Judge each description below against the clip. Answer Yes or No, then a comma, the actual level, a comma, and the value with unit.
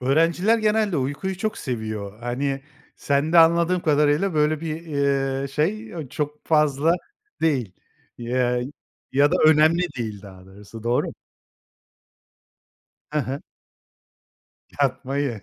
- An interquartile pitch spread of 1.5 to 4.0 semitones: No, average, 4.5 semitones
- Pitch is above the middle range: No, medium, 145 Hz